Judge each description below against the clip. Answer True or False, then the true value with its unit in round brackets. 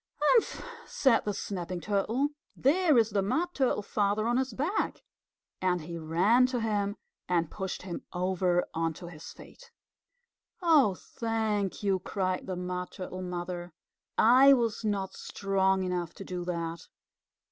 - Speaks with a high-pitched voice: True (195 Hz)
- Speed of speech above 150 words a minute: False (145 wpm)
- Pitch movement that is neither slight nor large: True (4.4 semitones)